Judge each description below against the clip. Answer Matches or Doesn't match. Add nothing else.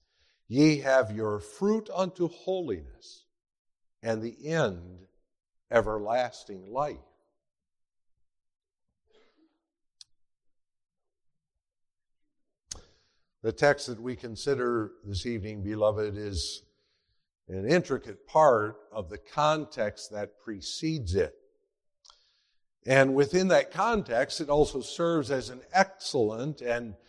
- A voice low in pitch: Matches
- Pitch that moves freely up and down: Matches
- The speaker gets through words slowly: Matches